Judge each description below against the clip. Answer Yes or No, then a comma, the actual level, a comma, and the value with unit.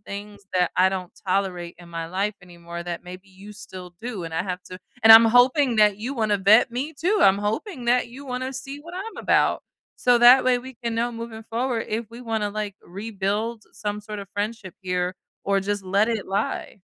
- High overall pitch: Yes, high, 210 Hz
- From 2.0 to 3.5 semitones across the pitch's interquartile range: No, average, 4.0 semitones